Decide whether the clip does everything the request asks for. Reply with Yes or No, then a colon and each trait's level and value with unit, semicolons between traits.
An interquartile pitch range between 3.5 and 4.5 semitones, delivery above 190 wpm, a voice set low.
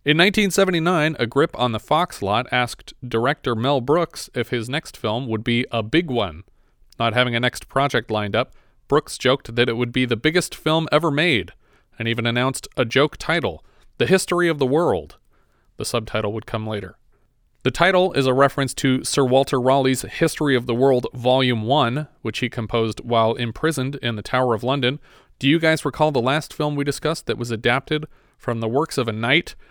Yes: average, 4.2 semitones; average, 200 wpm; low, 130 Hz